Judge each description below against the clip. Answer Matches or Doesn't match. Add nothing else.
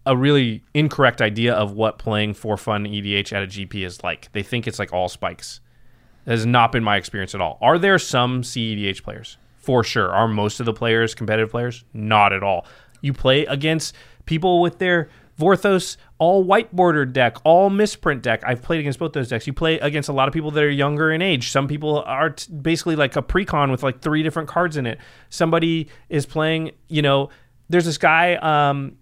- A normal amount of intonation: Doesn't match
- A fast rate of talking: Matches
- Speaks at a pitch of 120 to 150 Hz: Matches